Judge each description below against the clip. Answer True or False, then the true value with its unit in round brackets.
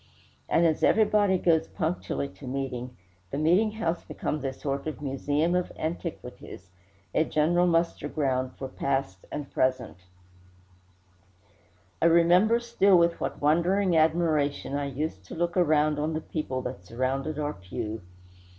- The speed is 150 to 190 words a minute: False (140 wpm)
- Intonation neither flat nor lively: True (4.2 semitones)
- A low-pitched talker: False (155 Hz)